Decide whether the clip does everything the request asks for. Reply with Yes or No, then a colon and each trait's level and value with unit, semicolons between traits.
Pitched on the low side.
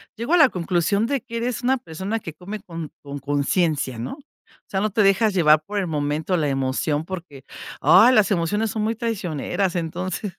No: medium, 185 Hz